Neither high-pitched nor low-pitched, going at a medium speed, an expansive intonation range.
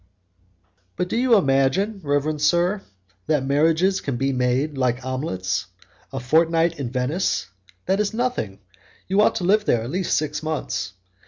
Yes: medium, 150 Hz; average, 155 wpm; wide, 5.9 semitones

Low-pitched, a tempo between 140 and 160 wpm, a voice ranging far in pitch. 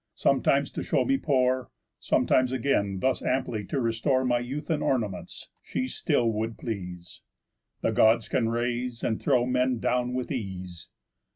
No: low, 120 Hz; average, 155 wpm; narrow, 2.6 semitones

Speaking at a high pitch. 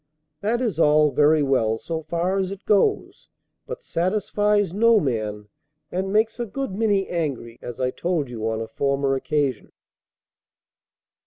No: medium, 165 Hz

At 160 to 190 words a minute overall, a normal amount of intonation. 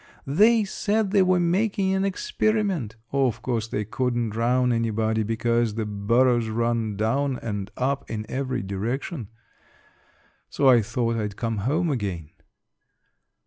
No: slow, 135 wpm; average, 5.0 semitones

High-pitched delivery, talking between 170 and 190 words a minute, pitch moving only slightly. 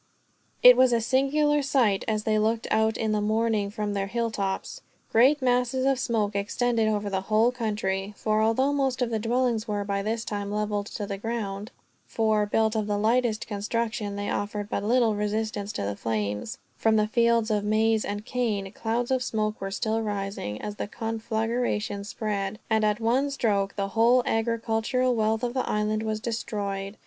Yes: high, 220 Hz; average, 180 wpm; narrow, 2.3 semitones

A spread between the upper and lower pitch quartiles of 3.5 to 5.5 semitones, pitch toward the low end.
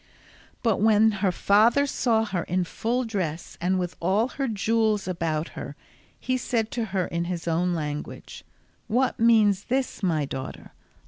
No: average, 4.5 semitones; high, 200 Hz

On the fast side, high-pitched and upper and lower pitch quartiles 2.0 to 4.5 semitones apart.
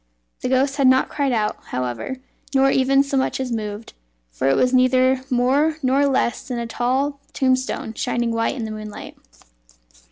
No: average, 170 wpm; very high, 255 Hz; average, 2.7 semitones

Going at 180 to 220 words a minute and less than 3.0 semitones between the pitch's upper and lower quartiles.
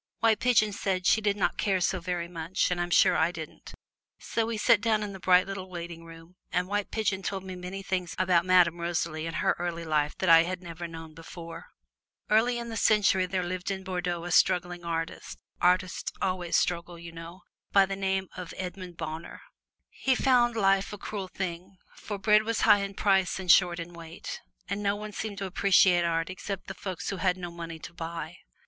Yes: fast, 205 wpm; narrow, 2.5 semitones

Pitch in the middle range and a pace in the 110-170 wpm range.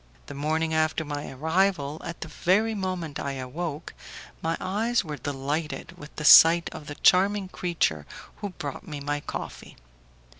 Yes: medium, 160 Hz; average, 155 wpm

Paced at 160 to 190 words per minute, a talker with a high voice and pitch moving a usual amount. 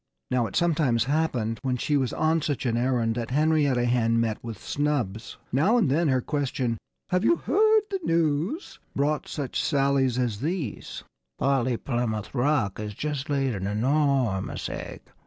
No: average, 165 wpm; low, 135 Hz; average, 4.4 semitones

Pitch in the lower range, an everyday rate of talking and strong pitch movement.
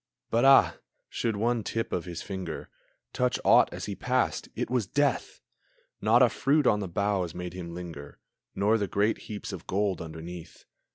No: low, 100 Hz; average, 175 wpm; average, 4.5 semitones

